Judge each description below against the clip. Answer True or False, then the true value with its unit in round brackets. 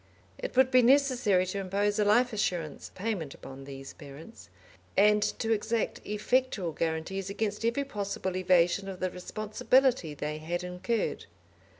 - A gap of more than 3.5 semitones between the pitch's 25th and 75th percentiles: True (4.2 semitones)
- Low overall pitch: False (200 Hz)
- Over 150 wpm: False (140 wpm)